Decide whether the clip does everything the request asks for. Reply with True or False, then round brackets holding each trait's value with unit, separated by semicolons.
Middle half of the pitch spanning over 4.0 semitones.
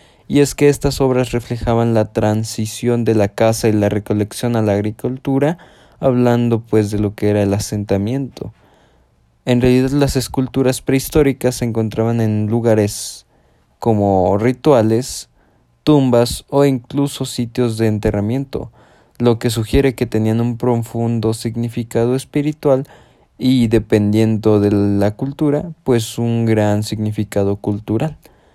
False (3.4 semitones)